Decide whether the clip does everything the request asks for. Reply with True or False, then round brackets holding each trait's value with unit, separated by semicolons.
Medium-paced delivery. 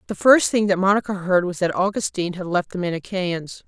False (215 wpm)